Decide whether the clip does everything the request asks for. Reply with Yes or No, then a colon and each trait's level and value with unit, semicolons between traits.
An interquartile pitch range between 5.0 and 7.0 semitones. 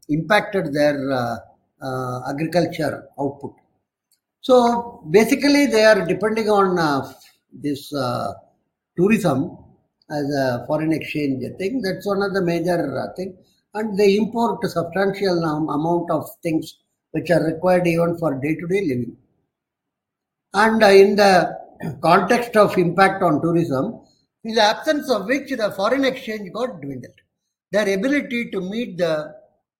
Yes: wide, 5.4 semitones